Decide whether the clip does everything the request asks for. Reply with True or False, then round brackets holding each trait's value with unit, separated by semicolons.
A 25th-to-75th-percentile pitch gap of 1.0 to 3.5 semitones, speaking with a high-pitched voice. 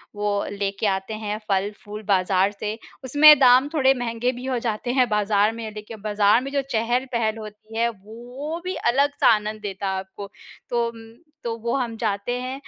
True (3.1 semitones; 225 Hz)